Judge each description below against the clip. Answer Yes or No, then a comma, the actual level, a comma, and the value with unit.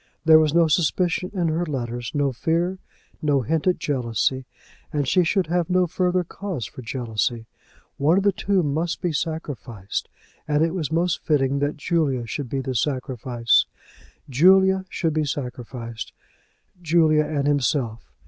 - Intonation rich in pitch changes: No, average, 4.8 semitones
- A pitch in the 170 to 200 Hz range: No, medium, 150 Hz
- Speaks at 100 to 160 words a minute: Yes, average, 155 wpm